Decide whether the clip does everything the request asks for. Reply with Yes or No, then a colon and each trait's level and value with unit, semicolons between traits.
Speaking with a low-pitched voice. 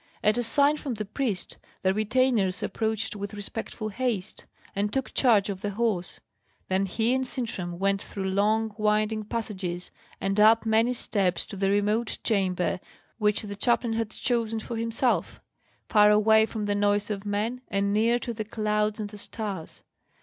No: high, 215 Hz